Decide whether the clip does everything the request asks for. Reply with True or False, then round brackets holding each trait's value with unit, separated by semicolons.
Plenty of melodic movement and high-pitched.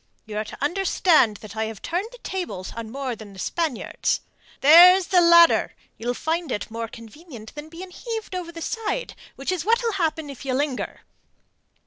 True (7.7 semitones; 315 Hz)